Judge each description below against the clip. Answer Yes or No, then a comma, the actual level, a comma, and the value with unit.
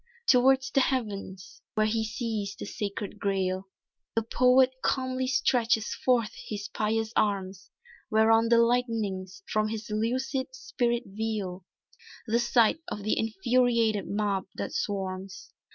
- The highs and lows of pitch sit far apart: No, average, 3.4 semitones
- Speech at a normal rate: No, slow, 125 wpm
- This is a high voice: Yes, high, 220 Hz